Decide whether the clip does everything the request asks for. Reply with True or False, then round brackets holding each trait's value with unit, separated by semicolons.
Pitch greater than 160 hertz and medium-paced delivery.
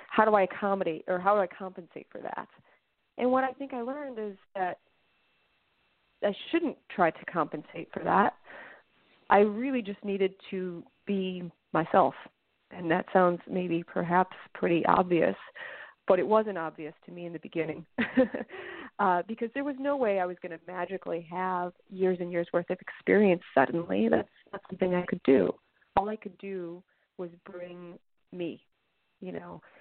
True (185 Hz; 165 wpm)